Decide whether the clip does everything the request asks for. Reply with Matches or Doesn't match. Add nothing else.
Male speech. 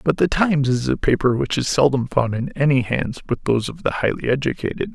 Matches